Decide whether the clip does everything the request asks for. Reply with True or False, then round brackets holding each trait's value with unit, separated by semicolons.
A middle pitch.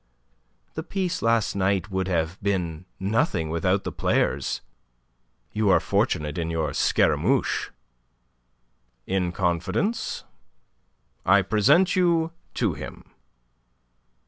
False (95 Hz)